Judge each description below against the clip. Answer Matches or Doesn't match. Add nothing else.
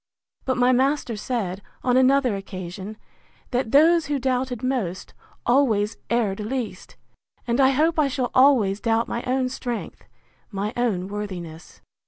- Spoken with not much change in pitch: Doesn't match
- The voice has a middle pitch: Doesn't match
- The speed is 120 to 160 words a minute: Matches